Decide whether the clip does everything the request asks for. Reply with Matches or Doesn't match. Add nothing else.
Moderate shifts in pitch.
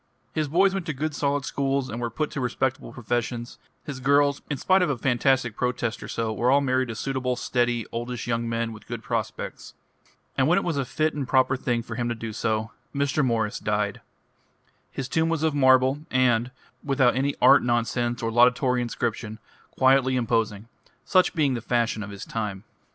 Matches